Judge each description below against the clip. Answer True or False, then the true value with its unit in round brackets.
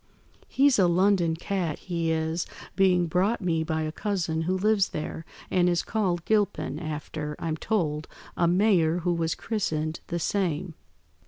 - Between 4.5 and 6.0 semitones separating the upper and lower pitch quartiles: False (3.2 semitones)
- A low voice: False (175 Hz)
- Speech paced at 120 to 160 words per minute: True (155 wpm)